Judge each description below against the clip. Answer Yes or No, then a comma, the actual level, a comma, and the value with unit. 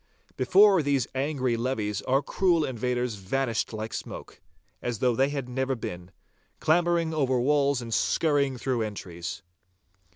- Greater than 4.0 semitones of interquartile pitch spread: No, average, 3.6 semitones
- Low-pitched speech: Yes, low, 130 Hz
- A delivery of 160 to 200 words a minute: No, slow, 135 wpm